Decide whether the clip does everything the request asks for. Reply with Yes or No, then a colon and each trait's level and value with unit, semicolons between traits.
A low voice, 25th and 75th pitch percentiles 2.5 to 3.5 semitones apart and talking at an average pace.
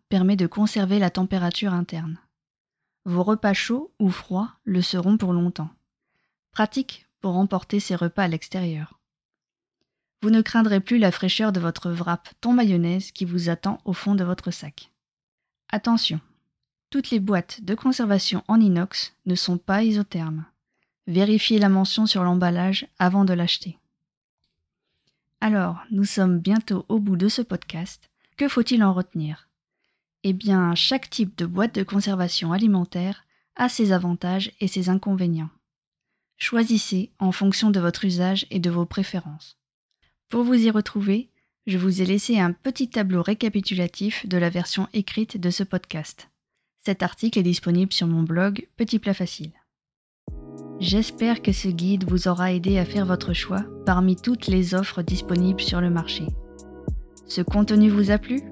No: high, 190 Hz; average, 3.0 semitones; average, 155 wpm